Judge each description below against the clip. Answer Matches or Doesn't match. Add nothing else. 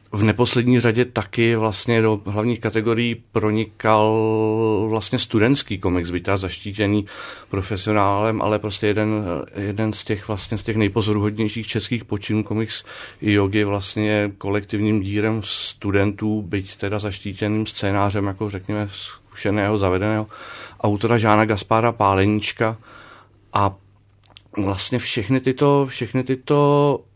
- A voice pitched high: Doesn't match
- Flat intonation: Matches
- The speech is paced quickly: Doesn't match